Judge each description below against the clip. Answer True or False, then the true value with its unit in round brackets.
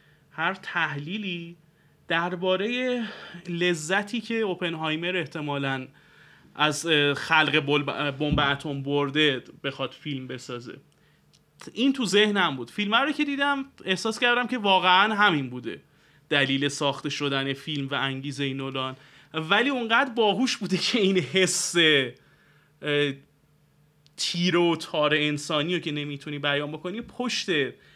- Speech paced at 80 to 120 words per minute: True (115 wpm)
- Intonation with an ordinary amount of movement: True (4.9 semitones)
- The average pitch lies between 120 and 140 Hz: False (155 Hz)